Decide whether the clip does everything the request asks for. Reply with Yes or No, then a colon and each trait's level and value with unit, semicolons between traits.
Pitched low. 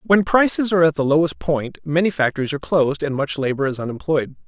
No: medium, 150 Hz